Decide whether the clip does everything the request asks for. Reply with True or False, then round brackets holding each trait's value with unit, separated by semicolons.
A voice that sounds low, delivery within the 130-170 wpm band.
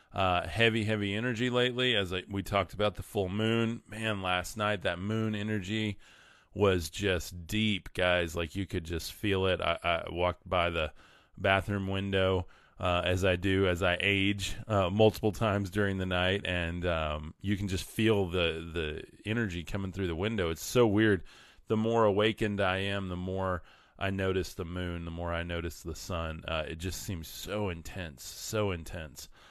False (95 Hz; 185 wpm)